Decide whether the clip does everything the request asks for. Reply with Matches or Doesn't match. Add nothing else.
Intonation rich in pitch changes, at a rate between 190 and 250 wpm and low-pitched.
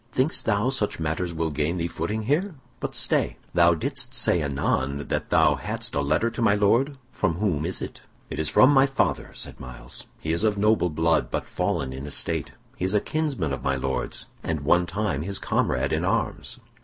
Matches